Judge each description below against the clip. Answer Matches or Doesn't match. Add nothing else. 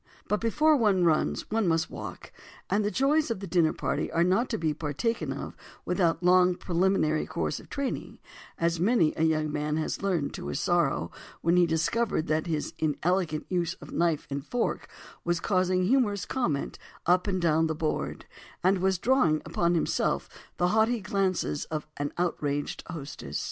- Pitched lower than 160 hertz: Doesn't match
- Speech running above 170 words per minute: Matches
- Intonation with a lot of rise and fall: Doesn't match